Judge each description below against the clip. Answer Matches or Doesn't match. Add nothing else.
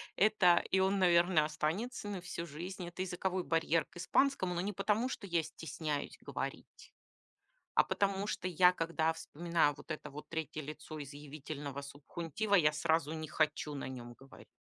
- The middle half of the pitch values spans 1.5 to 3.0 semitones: Doesn't match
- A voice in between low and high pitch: Matches